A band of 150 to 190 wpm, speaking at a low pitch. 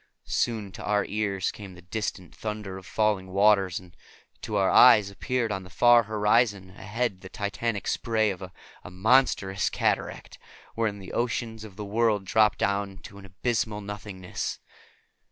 Yes: average, 155 wpm; low, 105 Hz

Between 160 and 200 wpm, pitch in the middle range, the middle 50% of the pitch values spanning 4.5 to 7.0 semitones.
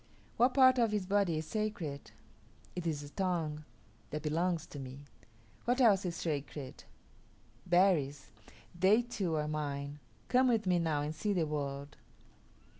No: average, 150 wpm; medium, 165 Hz; wide, 5.5 semitones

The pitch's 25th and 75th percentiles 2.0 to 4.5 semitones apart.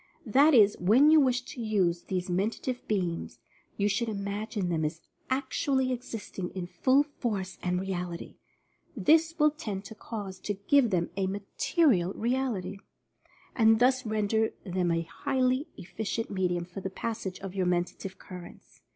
No: wide, 5.5 semitones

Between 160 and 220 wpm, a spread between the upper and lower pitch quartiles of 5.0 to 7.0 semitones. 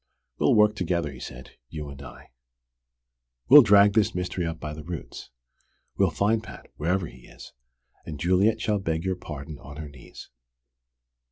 Yes: average, 165 wpm; average, 5.3 semitones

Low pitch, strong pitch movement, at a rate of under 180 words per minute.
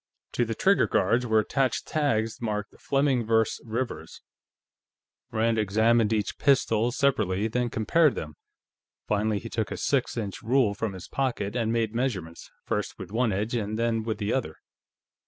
No: low, 115 Hz; average, 2.7 semitones; average, 160 wpm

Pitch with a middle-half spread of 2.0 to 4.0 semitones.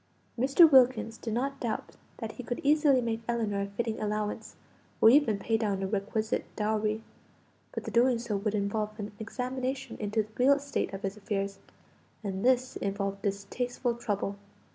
Yes: average, 3.5 semitones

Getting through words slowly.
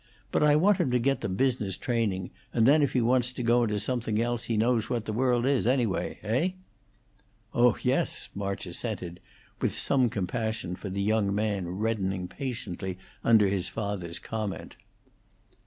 No: average, 170 wpm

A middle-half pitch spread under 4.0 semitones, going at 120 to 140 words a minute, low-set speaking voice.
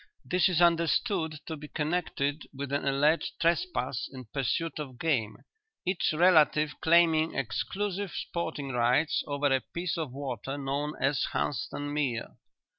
No: average, 3.4 semitones; slow, 135 wpm; medium, 150 Hz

